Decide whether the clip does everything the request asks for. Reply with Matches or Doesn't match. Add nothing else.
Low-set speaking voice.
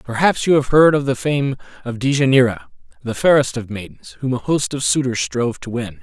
Matches